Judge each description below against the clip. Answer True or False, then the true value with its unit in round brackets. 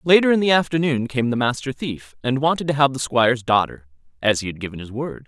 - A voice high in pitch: False (130 Hz)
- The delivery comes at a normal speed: False (240 wpm)